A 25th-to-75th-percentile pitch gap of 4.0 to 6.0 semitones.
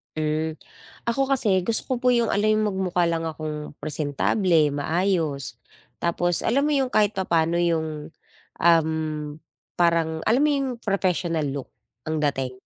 Yes: average, 5.1 semitones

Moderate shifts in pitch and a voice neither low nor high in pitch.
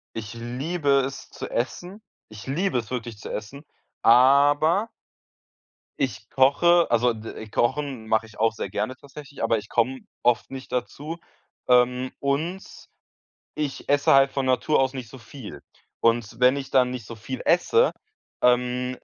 No: average, 3.5 semitones; low, 130 Hz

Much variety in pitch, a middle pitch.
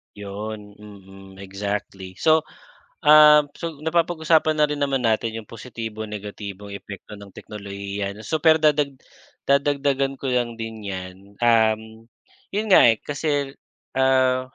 No: wide, 5.9 semitones; low, 115 Hz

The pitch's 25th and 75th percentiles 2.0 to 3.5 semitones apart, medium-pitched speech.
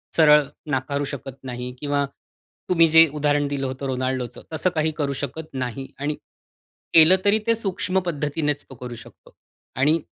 Yes: average, 3.2 semitones; medium, 145 Hz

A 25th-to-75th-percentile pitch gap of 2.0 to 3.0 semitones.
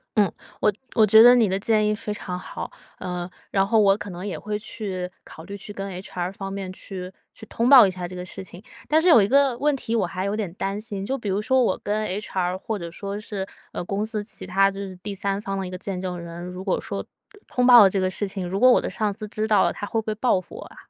Yes: narrow, 2.6 semitones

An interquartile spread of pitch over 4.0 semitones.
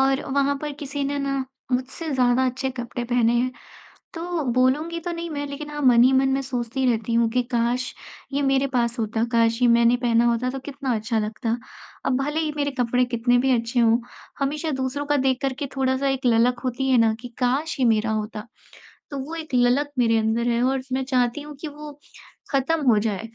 No: average, 3.0 semitones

